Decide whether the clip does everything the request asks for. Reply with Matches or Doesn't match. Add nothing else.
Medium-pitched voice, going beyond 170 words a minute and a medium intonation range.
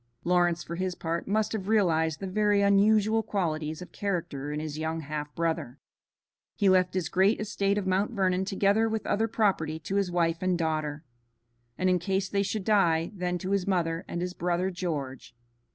Matches